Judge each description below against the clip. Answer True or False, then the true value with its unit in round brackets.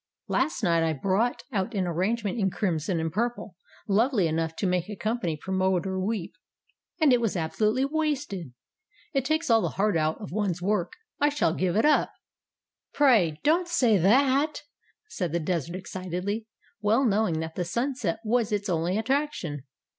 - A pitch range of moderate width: False (5.7 semitones)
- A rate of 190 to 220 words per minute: False (165 wpm)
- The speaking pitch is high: True (200 Hz)